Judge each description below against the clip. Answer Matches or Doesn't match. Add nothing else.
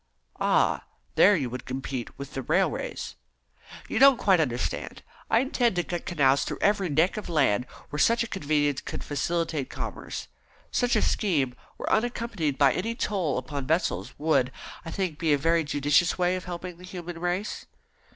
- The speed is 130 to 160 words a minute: Doesn't match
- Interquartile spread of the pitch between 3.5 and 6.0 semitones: Matches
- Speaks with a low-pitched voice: Doesn't match